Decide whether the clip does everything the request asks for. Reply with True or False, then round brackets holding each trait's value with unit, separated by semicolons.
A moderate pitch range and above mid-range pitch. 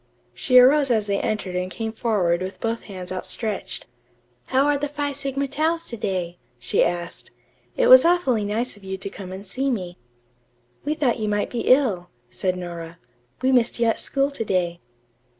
False (6.7 semitones; 220 Hz)